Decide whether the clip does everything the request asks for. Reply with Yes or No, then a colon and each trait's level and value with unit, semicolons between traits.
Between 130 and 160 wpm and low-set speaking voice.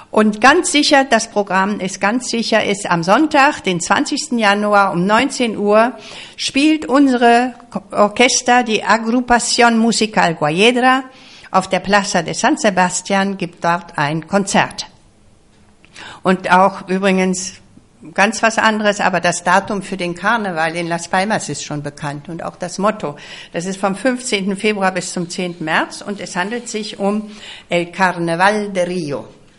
No: average, 150 wpm; high, 200 Hz